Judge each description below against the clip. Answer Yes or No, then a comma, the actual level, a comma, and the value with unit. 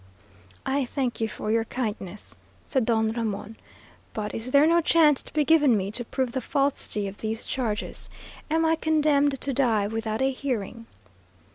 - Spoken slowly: No, average, 170 wpm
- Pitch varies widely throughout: No, average, 4.3 semitones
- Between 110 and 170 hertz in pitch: No, high, 245 Hz